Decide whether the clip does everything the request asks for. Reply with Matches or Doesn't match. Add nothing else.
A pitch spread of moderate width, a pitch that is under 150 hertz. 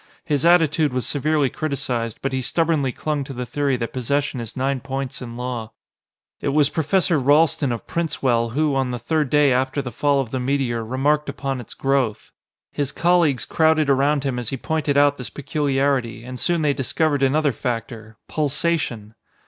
Matches